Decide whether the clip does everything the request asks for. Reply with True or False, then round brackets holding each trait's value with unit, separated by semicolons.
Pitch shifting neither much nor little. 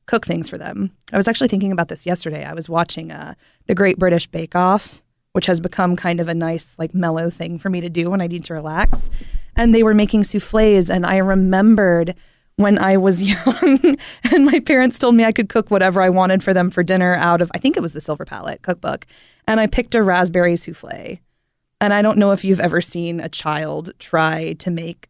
True (3.5 semitones)